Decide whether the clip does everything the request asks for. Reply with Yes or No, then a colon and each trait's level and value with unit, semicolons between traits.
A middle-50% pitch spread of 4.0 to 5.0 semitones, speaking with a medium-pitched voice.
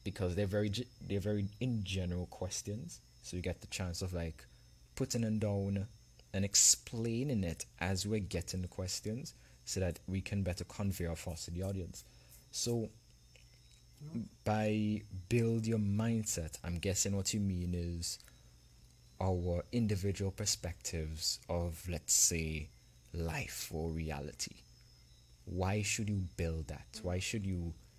No: average, 4.7 semitones; very low, 90 Hz